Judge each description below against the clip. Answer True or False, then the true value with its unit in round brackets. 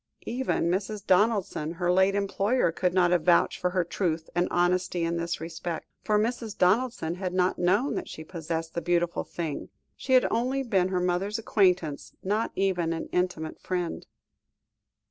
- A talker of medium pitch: True (180 Hz)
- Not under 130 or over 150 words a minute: False (165 wpm)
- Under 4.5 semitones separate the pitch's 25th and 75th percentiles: True (2.9 semitones)